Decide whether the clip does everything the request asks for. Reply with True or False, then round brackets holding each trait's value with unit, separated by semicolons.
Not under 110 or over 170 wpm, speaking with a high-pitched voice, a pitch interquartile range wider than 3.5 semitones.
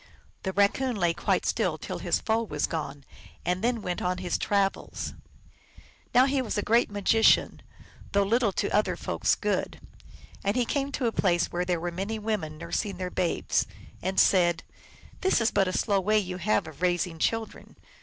False (190 wpm; 195 Hz; 3.9 semitones)